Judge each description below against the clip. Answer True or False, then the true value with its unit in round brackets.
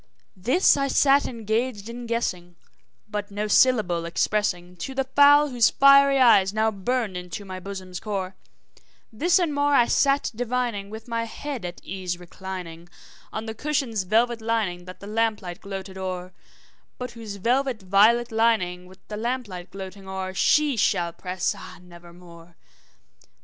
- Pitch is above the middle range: True (210 Hz)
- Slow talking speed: False (155 wpm)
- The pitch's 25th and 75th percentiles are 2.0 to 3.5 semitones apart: False (4.8 semitones)